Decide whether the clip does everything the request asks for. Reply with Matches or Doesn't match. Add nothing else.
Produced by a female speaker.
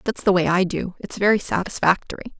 Matches